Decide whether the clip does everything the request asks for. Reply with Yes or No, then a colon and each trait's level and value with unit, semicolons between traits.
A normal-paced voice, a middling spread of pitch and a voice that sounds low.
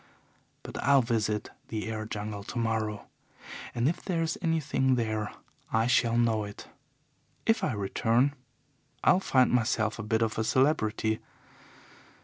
No: slow, 130 wpm; average, 3.4 semitones; low, 115 Hz